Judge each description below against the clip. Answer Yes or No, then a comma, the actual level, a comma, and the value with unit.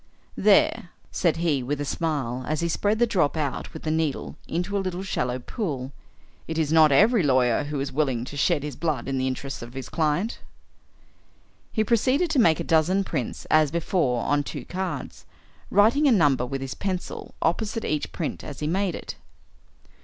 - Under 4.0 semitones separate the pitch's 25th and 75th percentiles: No, wide, 5.5 semitones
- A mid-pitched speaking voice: Yes, medium, 155 Hz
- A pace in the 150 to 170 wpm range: No, average, 190 wpm